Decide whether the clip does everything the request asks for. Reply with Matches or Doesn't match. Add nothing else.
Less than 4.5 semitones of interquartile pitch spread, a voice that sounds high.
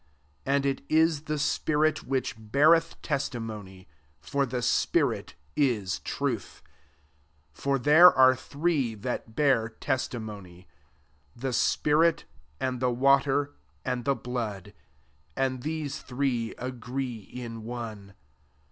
Doesn't match